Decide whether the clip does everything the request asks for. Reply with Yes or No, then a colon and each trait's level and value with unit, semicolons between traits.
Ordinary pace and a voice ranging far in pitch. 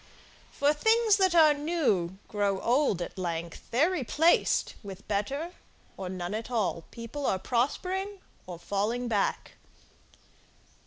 No: slow, 125 wpm; wide, 8.2 semitones